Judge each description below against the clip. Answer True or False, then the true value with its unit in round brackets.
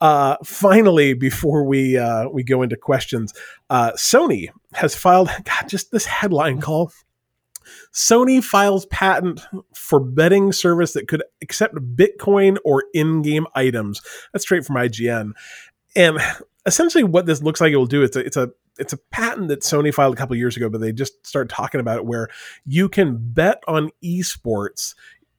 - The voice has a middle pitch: True (150 Hz)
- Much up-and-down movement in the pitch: True (6.5 semitones)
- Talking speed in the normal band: True (170 wpm)